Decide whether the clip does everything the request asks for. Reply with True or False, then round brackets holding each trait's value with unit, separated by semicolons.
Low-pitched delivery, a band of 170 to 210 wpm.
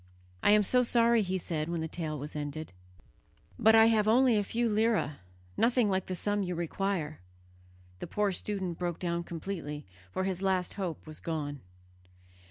False (185 Hz; 175 wpm)